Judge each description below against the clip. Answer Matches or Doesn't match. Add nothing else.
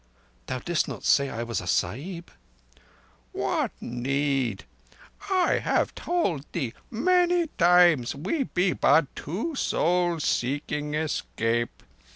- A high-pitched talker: Doesn't match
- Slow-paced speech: Matches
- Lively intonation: Matches